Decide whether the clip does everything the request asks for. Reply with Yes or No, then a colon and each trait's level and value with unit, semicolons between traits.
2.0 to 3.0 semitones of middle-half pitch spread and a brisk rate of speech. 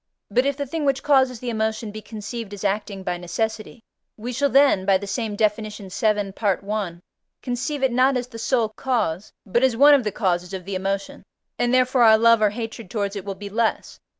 No: average, 3.8 semitones; fast, 215 wpm